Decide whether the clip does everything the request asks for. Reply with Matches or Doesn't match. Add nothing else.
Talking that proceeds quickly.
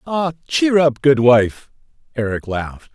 Doesn't match